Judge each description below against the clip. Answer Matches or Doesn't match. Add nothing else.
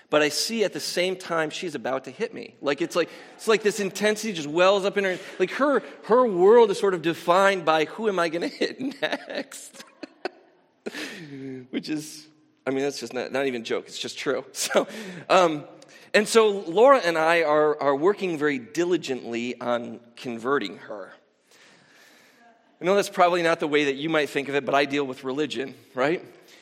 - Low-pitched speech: Doesn't match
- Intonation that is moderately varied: Doesn't match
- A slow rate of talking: Doesn't match